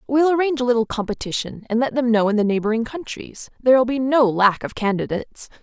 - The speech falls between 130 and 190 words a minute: No, fast, 205 wpm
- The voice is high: Yes, high, 235 Hz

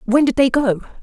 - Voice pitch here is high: Yes, very high, 255 Hz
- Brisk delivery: Yes, fast, 235 wpm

